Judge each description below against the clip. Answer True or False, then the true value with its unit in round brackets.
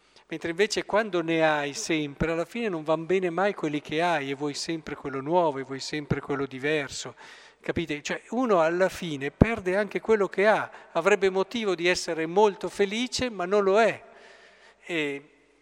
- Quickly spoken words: True (175 wpm)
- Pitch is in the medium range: True (175 Hz)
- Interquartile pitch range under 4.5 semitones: False (5.1 semitones)